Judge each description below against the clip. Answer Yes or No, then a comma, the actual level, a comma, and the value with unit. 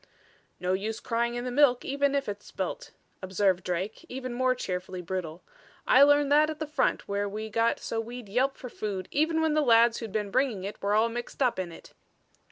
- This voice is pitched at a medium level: No, high, 230 Hz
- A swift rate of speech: Yes, fast, 210 wpm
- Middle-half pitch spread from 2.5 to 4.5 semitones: No, average, 5.0 semitones